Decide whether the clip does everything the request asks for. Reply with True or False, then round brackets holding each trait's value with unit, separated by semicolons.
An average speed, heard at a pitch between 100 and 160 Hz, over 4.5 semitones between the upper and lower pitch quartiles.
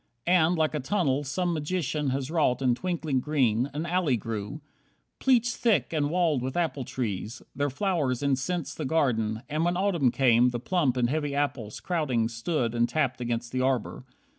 True (175 wpm; 140 Hz; 4.9 semitones)